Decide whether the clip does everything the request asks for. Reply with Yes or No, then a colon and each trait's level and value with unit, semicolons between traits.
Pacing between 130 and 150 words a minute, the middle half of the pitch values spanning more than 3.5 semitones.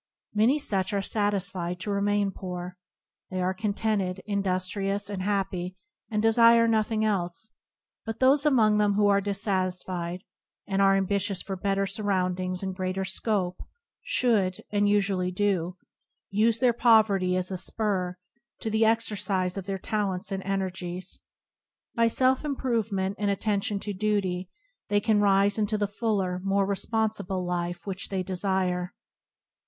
No: average, 145 wpm; narrow, 2.4 semitones